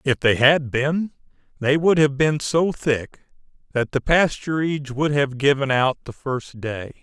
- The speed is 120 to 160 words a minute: No, average, 170 wpm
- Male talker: Yes, male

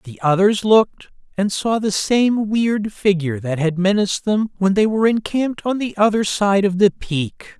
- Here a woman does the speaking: No, male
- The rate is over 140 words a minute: Yes, average, 190 wpm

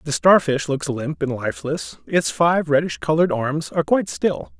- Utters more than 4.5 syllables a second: Yes, 5.1 syllables/s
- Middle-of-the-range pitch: Yes, medium, 145 Hz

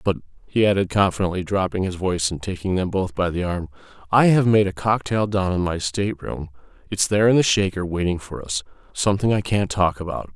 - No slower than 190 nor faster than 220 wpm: Yes, fast, 205 wpm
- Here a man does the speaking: Yes, male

